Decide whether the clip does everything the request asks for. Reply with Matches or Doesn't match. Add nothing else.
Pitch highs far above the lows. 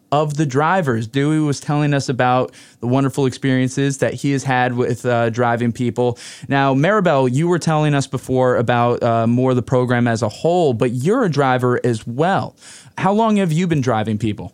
Doesn't match